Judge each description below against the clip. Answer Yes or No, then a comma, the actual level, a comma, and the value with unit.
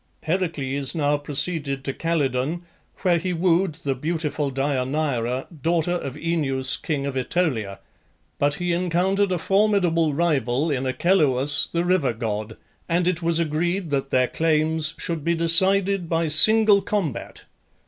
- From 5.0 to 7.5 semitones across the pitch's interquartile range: No, average, 4.0 semitones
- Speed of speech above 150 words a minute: No, average, 140 wpm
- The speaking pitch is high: No, medium, 160 Hz